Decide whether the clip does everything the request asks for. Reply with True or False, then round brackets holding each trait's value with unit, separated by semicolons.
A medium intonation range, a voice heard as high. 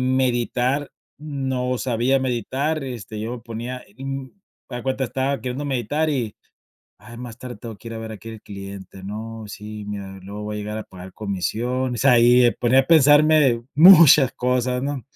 False (3.3 semitones; 125 Hz)